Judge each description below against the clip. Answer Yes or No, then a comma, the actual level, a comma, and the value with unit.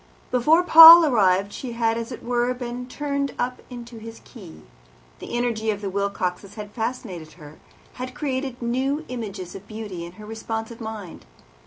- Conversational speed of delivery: Yes, average, 165 wpm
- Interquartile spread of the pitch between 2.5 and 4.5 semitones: Yes, average, 3.8 semitones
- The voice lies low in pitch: No, high, 230 Hz